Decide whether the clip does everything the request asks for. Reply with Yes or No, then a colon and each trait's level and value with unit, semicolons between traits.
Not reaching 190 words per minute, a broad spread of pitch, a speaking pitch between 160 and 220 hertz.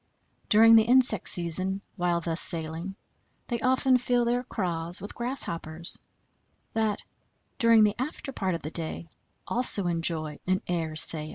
Yes: average, 150 wpm; wide, 5.7 semitones; medium, 185 Hz